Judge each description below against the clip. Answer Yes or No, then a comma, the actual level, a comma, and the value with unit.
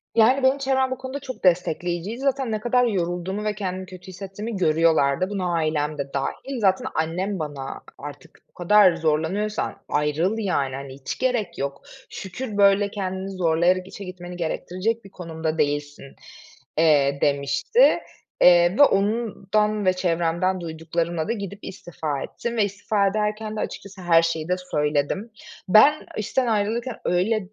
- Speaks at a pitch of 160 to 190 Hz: Yes, medium, 185 Hz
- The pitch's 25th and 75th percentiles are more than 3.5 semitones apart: Yes, average, 4.6 semitones